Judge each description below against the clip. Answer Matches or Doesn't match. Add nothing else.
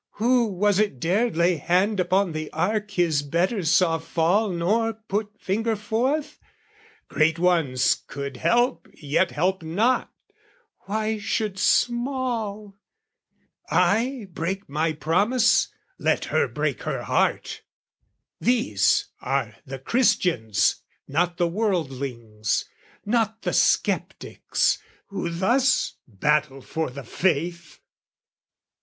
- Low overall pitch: Doesn't match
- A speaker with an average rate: Doesn't match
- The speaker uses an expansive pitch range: Matches